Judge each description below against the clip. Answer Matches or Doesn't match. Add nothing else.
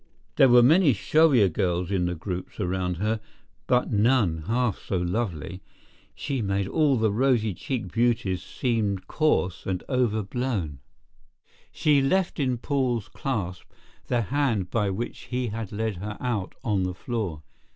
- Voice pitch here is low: Matches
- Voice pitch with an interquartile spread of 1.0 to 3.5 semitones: Doesn't match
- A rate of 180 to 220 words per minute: Doesn't match